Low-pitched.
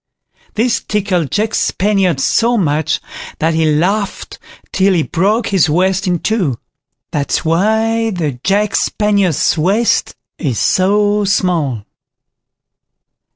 No: high, 190 Hz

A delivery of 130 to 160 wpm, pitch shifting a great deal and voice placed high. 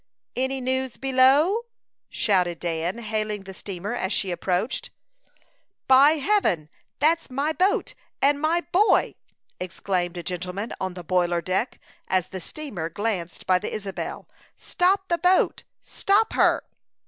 Yes: slow, 135 wpm; wide, 8.2 semitones; high, 215 Hz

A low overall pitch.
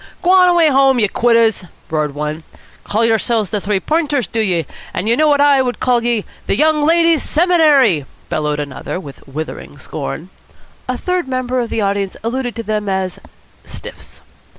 No: high, 230 Hz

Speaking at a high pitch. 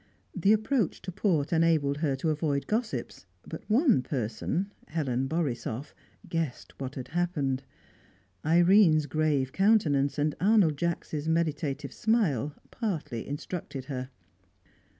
No: medium, 155 Hz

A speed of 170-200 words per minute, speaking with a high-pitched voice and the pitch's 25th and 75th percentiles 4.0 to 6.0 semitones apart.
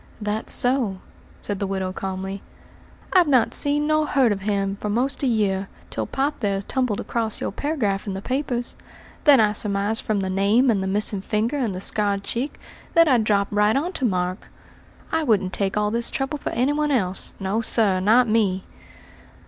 Yes: average, 190 wpm; high, 215 Hz; average, 4.7 semitones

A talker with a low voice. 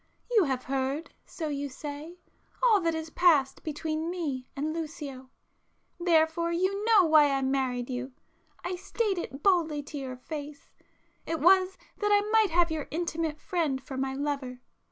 No: very high, 310 Hz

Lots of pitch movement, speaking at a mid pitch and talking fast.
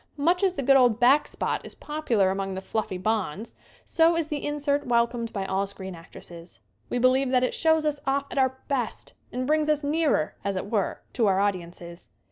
No: wide, 6.8 semitones; high, 245 Hz; fast, 210 wpm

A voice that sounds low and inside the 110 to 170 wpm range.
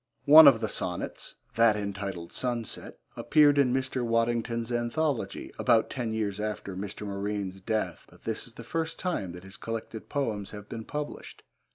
Yes: low, 115 Hz; average, 165 wpm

